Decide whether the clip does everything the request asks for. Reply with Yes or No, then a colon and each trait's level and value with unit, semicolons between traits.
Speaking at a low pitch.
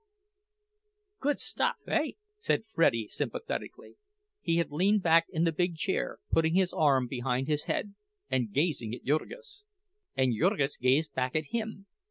No: medium, 160 Hz